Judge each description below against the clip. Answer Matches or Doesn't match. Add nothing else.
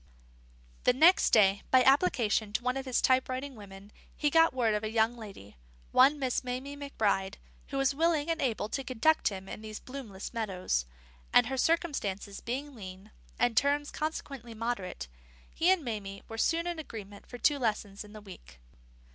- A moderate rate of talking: Matches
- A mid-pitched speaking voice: Doesn't match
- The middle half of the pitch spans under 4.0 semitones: Doesn't match